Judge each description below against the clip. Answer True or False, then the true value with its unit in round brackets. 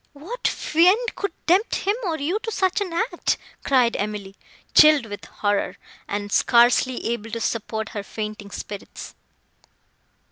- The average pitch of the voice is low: False (250 Hz)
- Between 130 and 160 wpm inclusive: True (140 wpm)